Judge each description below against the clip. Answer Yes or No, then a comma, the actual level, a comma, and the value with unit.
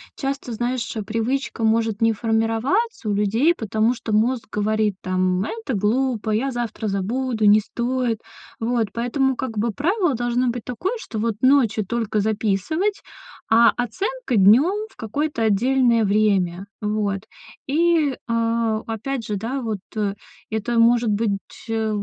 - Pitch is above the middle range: Yes, high, 230 Hz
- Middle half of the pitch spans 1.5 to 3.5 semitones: Yes, average, 3.2 semitones